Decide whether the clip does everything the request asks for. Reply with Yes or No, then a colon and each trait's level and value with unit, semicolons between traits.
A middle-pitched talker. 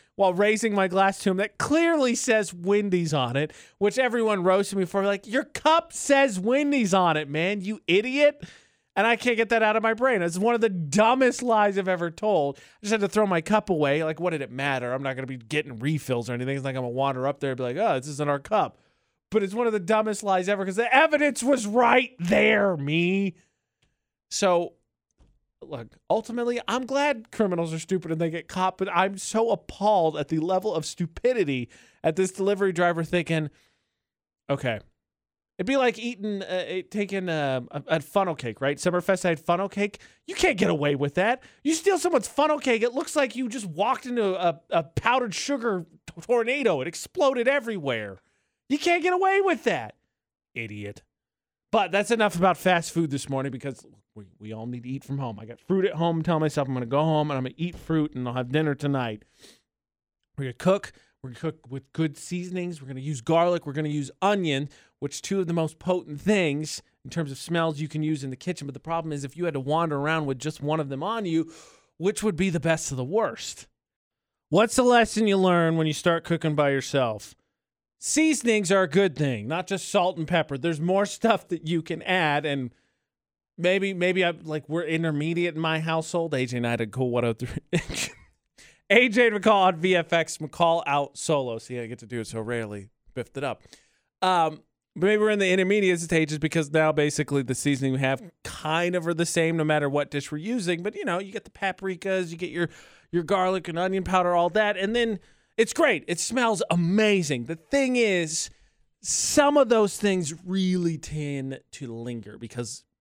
Yes: medium, 175 Hz